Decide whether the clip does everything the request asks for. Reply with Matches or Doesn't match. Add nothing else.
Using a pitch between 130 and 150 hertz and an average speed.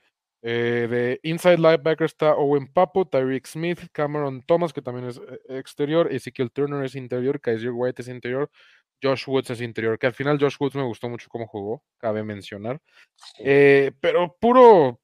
Matches